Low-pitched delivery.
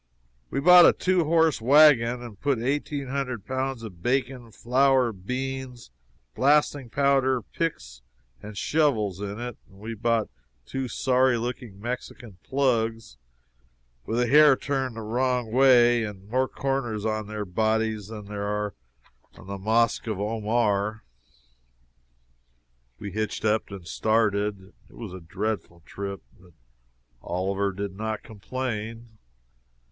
Yes: low, 115 Hz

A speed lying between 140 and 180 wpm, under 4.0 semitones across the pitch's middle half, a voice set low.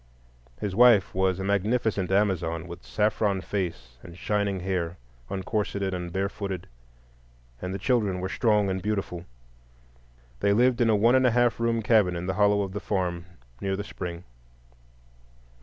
Yes: average, 155 wpm; narrow, 2.5 semitones; low, 100 Hz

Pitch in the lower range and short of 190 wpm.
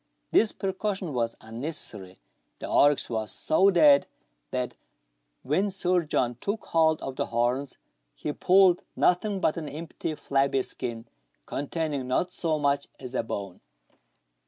No: medium, 145 Hz; average, 140 wpm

